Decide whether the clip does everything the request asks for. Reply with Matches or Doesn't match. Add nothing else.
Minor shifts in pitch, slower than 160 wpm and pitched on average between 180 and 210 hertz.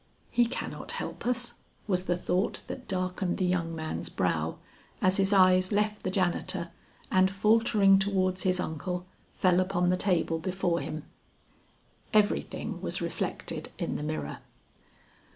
Matches